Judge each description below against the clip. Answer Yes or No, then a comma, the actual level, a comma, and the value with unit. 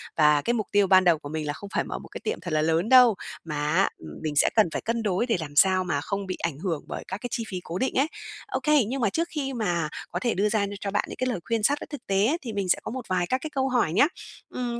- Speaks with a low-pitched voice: No, high, 200 Hz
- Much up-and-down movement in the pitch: Yes, wide, 6.1 semitones